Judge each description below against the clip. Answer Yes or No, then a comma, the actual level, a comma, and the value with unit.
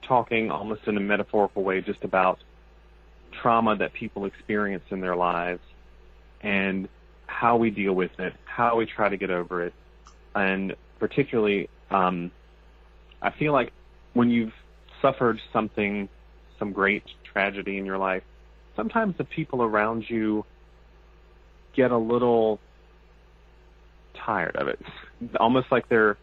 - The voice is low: Yes, very low, 95 Hz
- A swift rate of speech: No, slow, 135 wpm